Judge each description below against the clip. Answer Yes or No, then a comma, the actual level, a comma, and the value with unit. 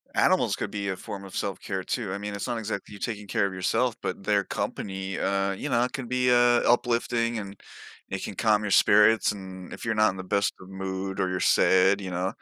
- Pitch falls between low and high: No, low, 100 Hz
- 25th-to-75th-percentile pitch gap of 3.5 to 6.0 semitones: No, average, 2.9 semitones